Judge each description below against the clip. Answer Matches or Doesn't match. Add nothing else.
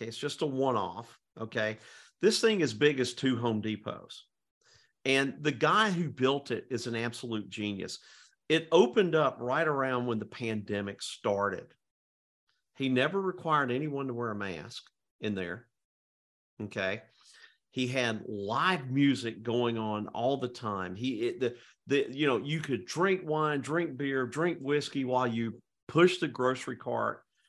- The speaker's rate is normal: Matches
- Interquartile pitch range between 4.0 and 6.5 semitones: Matches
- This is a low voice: Matches